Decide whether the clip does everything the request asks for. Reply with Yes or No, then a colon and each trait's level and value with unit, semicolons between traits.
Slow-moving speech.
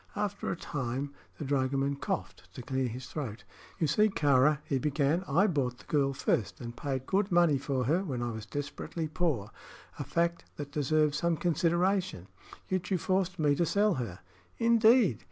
No: average, 175 wpm